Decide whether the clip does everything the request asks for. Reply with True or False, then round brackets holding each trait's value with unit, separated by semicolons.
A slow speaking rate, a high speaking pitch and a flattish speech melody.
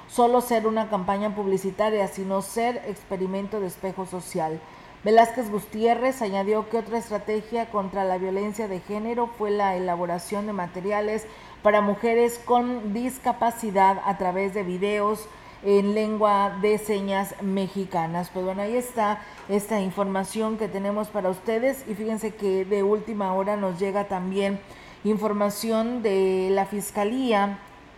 False (135 wpm; 205 Hz; 2.1 semitones)